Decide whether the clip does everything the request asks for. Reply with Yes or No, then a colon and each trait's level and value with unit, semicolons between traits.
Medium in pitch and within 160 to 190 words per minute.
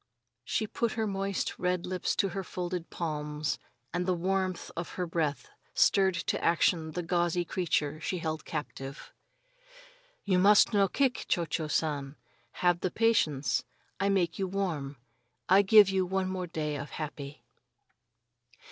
No: medium, 175 Hz; average, 150 wpm